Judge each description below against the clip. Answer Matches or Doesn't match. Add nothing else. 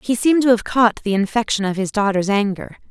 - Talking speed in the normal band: Doesn't match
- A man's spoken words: Doesn't match